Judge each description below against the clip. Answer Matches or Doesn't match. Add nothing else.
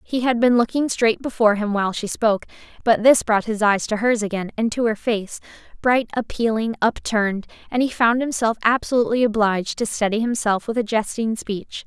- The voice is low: Doesn't match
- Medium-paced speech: Matches